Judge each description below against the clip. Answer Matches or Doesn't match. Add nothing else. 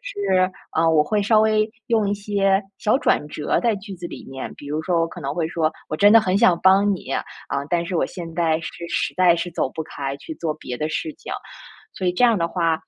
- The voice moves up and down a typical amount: Matches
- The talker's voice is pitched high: Doesn't match